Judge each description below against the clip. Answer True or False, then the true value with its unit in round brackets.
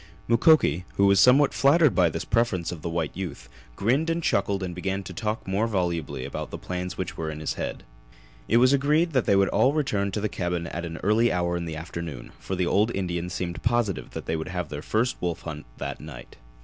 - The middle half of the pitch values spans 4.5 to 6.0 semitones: True (5.3 semitones)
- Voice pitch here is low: True (95 Hz)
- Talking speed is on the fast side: True (225 wpm)